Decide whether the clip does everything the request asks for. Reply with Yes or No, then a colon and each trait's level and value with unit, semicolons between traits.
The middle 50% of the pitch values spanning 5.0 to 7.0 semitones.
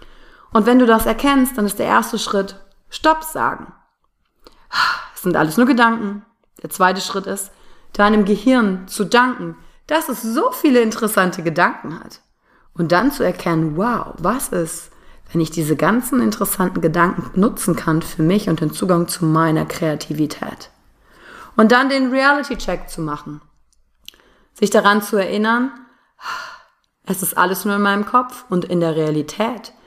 Yes: wide, 5.6 semitones